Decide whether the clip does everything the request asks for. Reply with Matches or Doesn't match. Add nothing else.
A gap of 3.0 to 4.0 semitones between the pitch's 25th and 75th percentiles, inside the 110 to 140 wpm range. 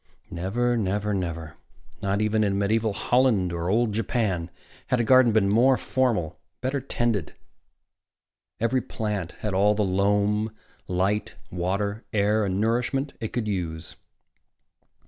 Matches